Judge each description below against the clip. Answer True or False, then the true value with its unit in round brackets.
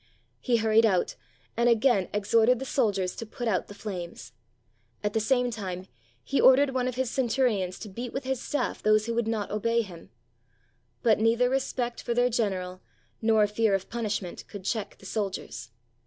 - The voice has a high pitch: True (225 Hz)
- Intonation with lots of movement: False (3.4 semitones)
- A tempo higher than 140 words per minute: True (185 wpm)